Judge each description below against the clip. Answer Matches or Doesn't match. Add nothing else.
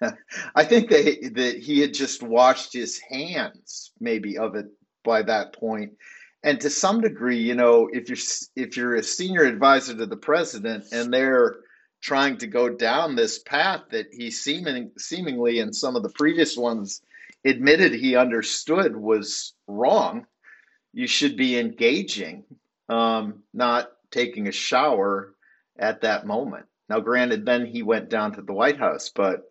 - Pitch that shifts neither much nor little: Matches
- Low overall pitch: Matches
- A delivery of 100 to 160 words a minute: Matches